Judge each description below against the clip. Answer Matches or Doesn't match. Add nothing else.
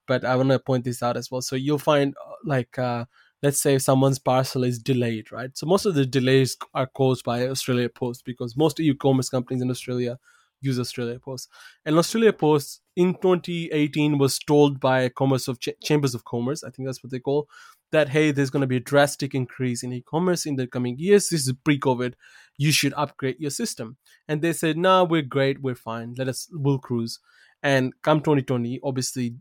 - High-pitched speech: Doesn't match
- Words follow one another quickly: Matches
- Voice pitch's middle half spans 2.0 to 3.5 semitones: Matches